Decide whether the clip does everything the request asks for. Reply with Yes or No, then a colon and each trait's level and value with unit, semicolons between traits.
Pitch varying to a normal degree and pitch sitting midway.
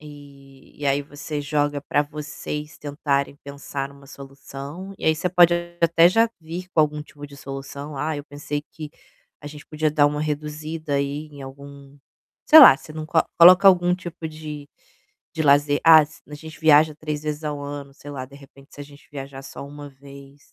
No: narrow, 1.7 semitones; medium, 145 Hz